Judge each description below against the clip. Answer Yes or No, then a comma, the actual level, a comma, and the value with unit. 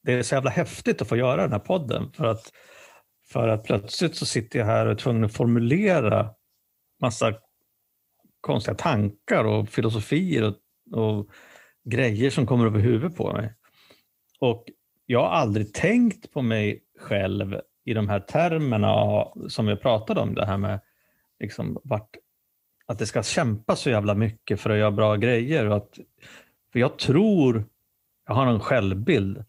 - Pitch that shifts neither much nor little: Yes, average, 3.8 semitones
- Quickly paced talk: No, average, 165 wpm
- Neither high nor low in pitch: No, low, 110 Hz